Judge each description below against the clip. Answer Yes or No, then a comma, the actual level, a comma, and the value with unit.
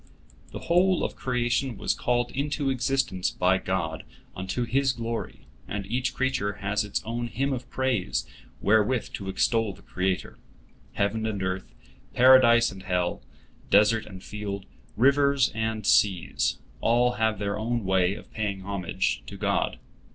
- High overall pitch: No, low, 110 Hz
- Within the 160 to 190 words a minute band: No, average, 145 wpm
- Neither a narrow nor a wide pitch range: Yes, average, 4.2 semitones